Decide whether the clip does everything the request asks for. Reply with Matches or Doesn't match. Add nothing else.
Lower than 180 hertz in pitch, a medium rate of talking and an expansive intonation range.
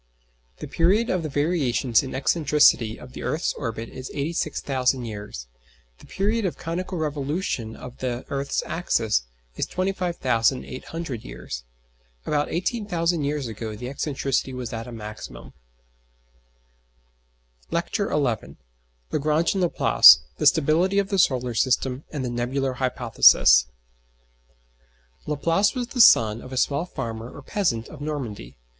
Doesn't match